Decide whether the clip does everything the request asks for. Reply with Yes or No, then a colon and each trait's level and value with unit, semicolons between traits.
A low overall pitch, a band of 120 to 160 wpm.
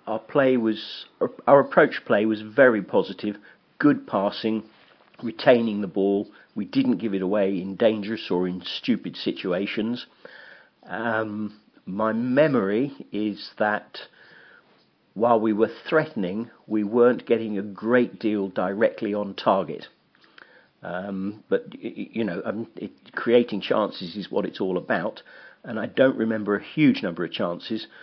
Yes: low, 110 Hz; average, 140 wpm